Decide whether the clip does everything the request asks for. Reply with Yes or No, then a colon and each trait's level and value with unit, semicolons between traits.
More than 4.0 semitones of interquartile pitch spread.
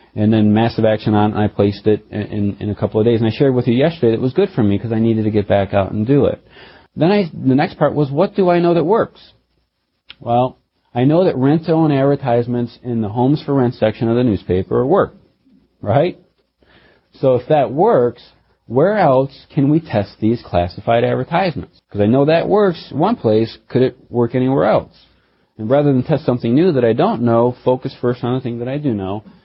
Yes: average, 4.4 semitones